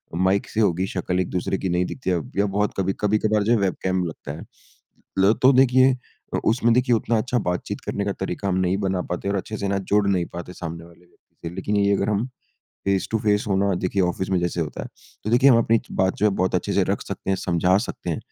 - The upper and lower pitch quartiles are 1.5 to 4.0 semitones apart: Yes, average, 2.8 semitones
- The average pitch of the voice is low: Yes, very low, 95 Hz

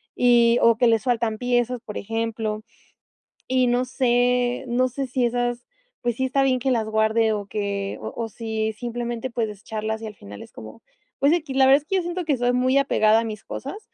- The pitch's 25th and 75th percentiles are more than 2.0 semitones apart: Yes, narrow, 2.6 semitones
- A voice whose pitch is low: No, high, 240 Hz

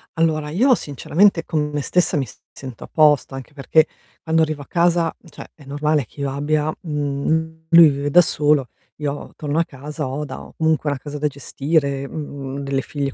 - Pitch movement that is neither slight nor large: No, narrow, 2.3 semitones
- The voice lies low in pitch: No, medium, 150 Hz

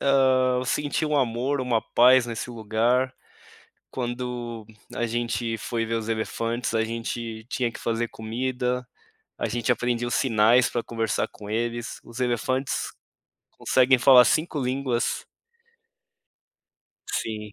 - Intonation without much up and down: Yes, narrow, 1.9 semitones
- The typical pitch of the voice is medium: No, low, 120 Hz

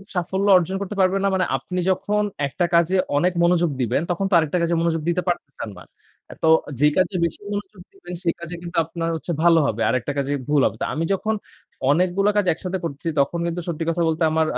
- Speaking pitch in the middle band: Yes, medium, 170 Hz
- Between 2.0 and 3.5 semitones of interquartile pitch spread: Yes, narrow, 2.6 semitones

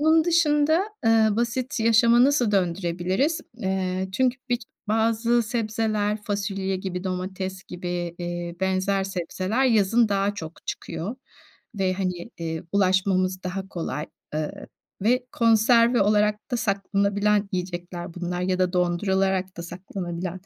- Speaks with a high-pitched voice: Yes, high, 195 Hz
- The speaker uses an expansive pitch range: No, average, 3.6 semitones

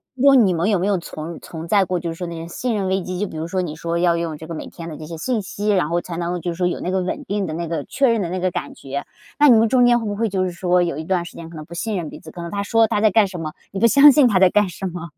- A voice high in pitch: No, medium, 180 Hz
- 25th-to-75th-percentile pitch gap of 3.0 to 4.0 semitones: Yes, average, 3.5 semitones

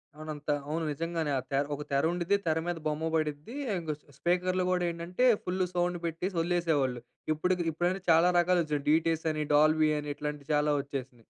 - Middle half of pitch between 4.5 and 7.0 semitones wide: No, average, 2.9 semitones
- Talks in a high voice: No, medium, 160 Hz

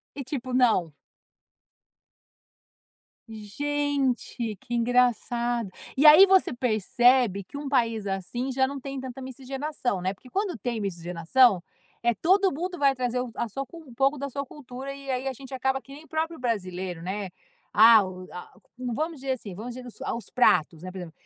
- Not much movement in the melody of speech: No, average, 4.2 semitones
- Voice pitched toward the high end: Yes, very high, 250 Hz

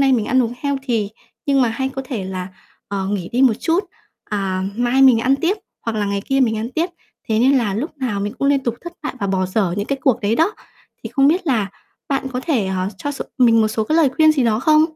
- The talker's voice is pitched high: Yes, high, 245 Hz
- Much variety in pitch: No, average, 4.8 semitones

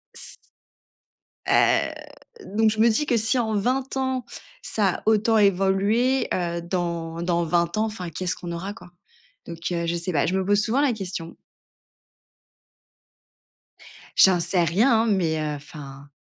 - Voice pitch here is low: No, high, 190 Hz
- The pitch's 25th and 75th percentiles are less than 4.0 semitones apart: No, average, 4.5 semitones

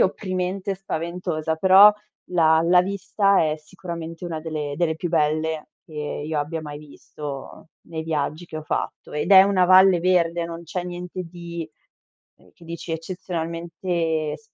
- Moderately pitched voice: Yes, medium, 170 Hz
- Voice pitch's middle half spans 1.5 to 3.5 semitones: Yes, narrow, 2.4 semitones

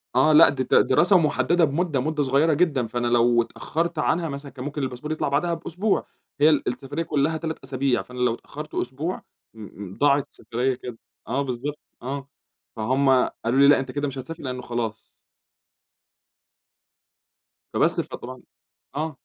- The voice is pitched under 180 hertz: Yes, medium, 140 Hz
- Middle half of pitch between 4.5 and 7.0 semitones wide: No, average, 3.6 semitones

